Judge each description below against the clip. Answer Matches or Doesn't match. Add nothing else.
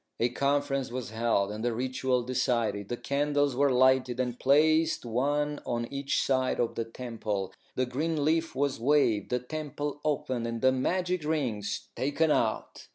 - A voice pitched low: Matches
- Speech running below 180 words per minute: Matches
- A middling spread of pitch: Matches